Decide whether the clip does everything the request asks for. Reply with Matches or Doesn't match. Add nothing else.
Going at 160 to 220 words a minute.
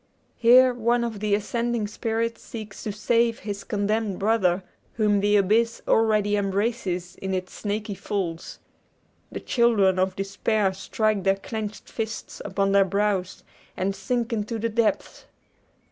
Doesn't match